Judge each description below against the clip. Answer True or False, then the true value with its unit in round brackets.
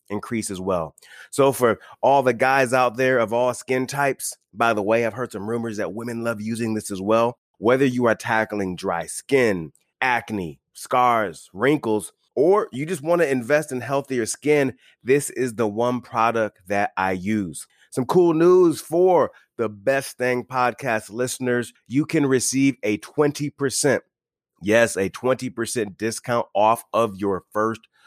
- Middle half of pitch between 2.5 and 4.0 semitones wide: True (3.6 semitones)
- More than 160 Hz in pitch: False (120 Hz)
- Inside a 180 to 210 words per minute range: False (160 wpm)